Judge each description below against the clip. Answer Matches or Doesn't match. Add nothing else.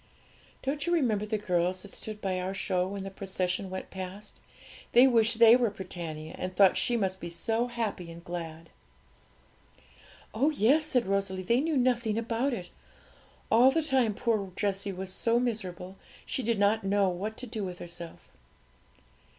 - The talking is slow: Doesn't match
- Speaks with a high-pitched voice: Matches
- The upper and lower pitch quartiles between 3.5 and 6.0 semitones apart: Matches